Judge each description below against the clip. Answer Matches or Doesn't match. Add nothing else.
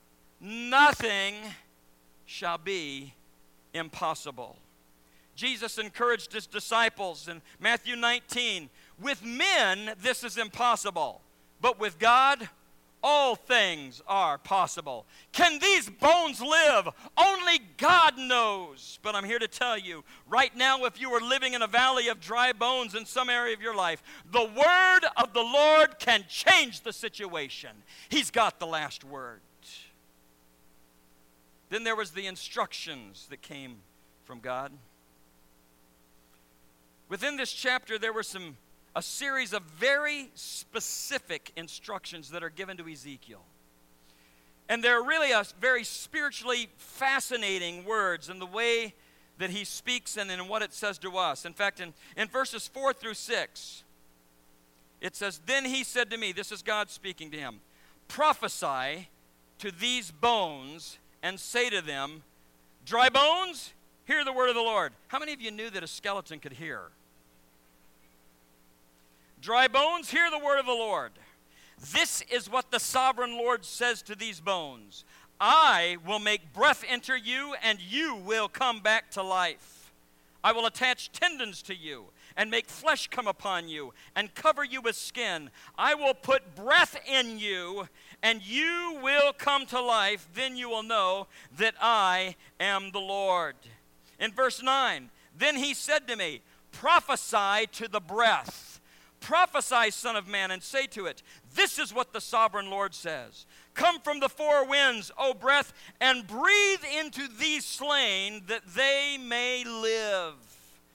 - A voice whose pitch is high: Matches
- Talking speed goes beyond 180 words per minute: Doesn't match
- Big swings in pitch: Matches